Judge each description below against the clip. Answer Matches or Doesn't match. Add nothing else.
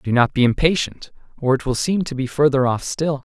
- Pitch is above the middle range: Doesn't match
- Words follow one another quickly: Matches